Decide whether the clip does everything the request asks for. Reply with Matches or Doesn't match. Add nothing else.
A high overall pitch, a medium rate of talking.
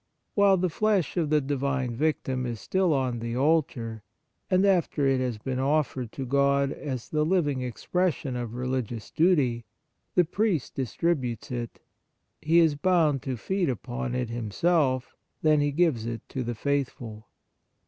Doesn't match